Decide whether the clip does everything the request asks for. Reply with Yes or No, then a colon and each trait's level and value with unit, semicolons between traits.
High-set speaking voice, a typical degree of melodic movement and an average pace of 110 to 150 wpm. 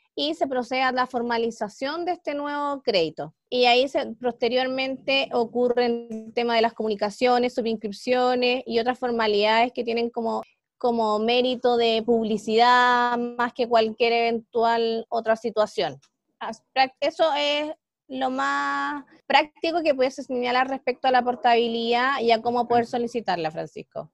No: high, 245 Hz; narrow, 2.2 semitones; average, 135 wpm